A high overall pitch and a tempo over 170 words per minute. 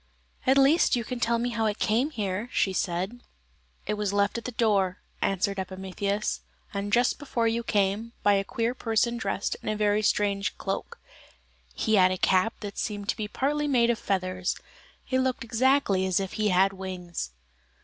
Yes: high, 210 Hz; average, 180 wpm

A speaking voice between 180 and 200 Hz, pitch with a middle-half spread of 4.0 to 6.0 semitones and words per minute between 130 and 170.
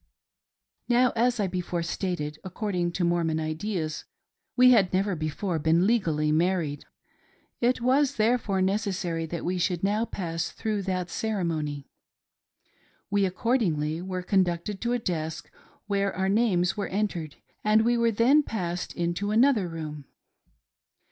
Yes: medium, 185 Hz; average, 4.3 semitones; average, 140 wpm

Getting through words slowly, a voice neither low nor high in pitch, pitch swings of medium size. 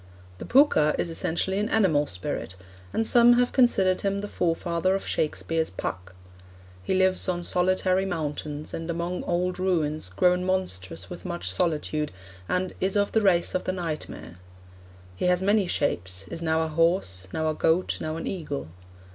No: average, 165 wpm; medium, 175 Hz; average, 3.6 semitones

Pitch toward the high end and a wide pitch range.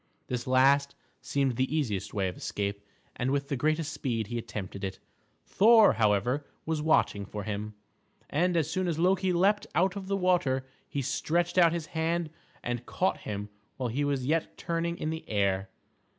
No: medium, 140 Hz; wide, 7.3 semitones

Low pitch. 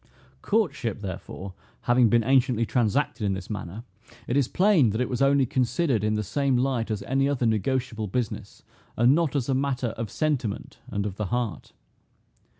Yes: low, 120 Hz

